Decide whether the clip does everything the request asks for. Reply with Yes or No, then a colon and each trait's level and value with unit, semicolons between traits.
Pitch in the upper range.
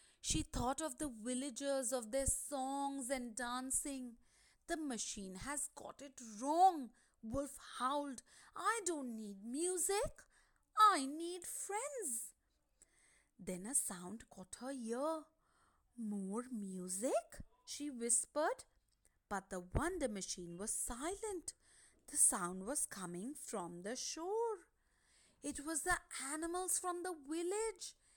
Yes: very high, 275 Hz